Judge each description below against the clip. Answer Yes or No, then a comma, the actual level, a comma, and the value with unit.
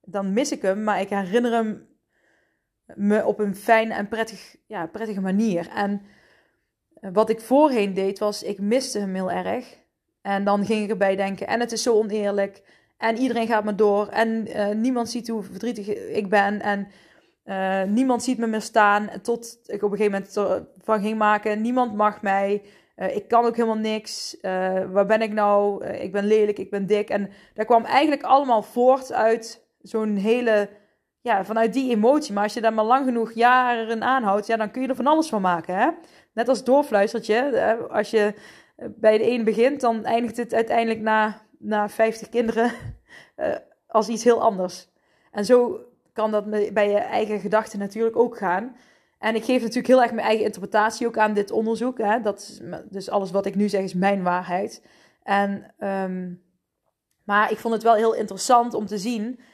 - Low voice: No, high, 215 Hz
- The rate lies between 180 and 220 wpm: Yes, average, 195 wpm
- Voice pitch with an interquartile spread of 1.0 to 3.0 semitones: Yes, narrow, 2.4 semitones